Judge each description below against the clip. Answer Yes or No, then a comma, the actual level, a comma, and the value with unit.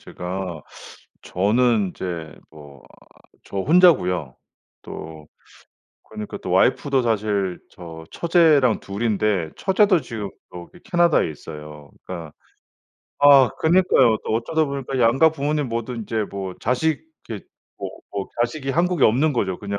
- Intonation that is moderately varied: No, wide, 7.7 semitones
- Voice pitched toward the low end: Yes, low, 110 Hz